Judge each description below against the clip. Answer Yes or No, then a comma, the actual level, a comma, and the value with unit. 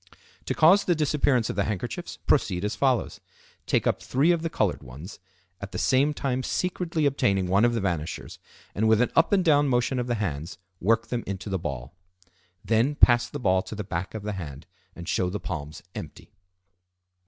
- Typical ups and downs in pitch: No, wide, 6.6 semitones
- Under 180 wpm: No, average, 200 wpm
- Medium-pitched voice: No, low, 110 Hz